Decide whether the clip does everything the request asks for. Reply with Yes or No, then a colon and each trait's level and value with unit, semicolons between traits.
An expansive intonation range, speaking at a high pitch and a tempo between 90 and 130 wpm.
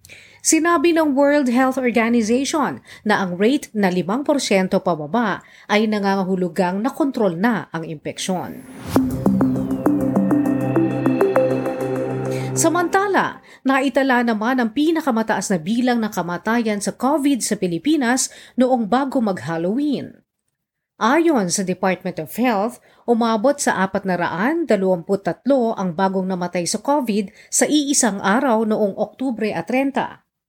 Yes: wide, 6.0 semitones; high, 220 Hz; slow, 110 wpm